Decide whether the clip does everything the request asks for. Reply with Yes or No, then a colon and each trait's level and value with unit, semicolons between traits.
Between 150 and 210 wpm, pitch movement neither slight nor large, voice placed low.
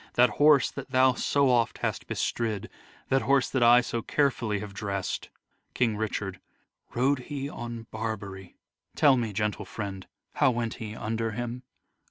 Yes: average, 160 wpm; average, 3.2 semitones; low, 115 Hz